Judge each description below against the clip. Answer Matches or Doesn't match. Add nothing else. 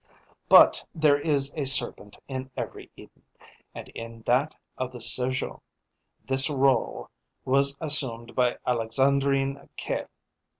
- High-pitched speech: Doesn't match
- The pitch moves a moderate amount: Doesn't match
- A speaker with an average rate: Doesn't match